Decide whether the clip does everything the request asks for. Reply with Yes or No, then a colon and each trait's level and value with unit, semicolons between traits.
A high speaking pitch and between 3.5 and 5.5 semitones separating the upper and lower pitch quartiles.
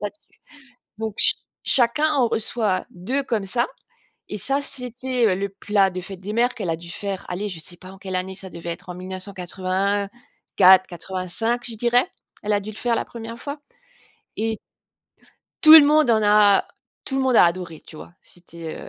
Yes: high, 205 Hz; average, 4.5 semitones